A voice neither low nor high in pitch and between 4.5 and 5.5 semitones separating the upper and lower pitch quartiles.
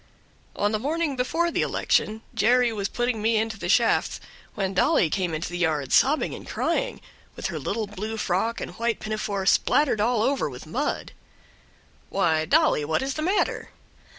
No: high, 220 Hz; average, 4.8 semitones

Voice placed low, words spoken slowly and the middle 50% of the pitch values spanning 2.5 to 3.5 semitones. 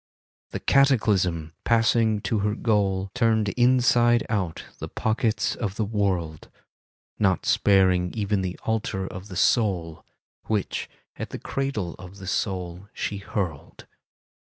Yes: low, 100 Hz; slow, 130 wpm; average, 3.2 semitones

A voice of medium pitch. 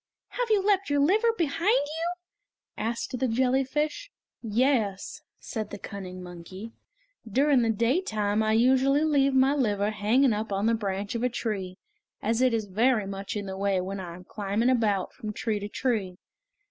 No: high, 225 Hz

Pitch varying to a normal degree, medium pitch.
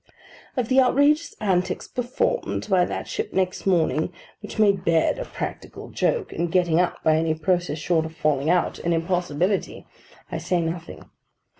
Yes: average, 3.8 semitones; medium, 180 Hz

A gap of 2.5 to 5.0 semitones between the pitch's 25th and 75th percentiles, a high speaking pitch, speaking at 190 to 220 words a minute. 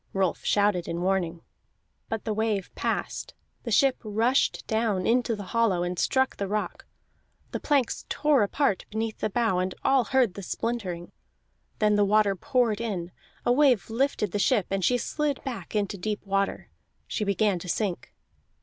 No: average, 3.7 semitones; high, 210 Hz; average, 170 wpm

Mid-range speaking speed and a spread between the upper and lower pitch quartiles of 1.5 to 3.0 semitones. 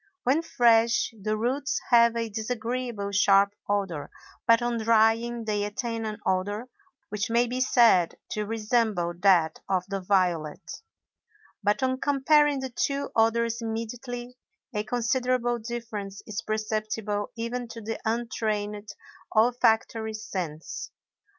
No: slow, 125 wpm; narrow, 2.6 semitones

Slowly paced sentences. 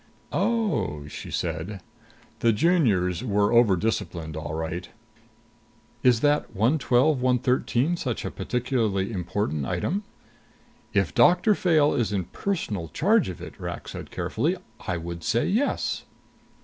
Yes: slow, 125 wpm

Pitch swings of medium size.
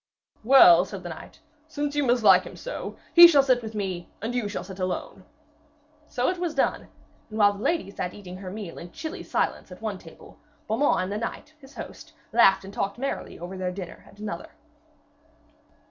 No: wide, 6.2 semitones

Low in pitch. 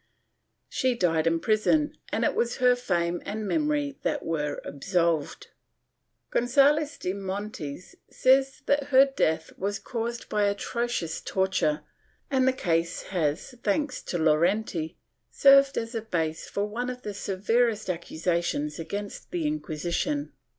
No: high, 205 Hz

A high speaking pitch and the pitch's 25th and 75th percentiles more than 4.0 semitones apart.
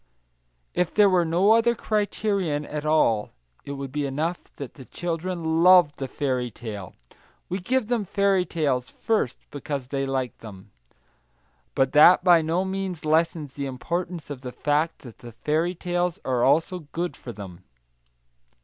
No: medium, 160 Hz; average, 5.0 semitones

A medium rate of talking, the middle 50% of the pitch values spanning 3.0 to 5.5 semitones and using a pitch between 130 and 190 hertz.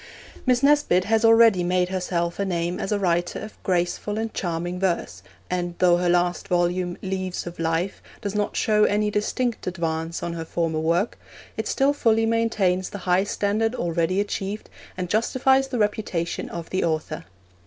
Yes: average, 170 wpm; average, 3.6 semitones; medium, 185 Hz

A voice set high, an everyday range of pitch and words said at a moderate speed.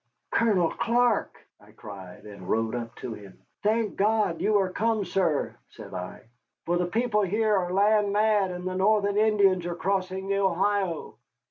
Yes: high, 195 Hz; average, 3.3 semitones; average, 165 wpm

